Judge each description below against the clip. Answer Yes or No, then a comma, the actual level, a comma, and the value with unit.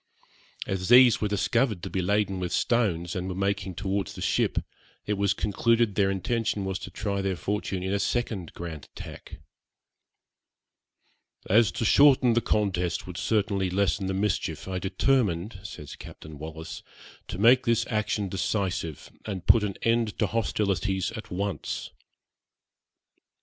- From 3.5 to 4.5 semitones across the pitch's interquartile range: No, narrow, 2.6 semitones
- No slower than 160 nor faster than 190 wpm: No, average, 150 wpm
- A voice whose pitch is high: No, low, 100 Hz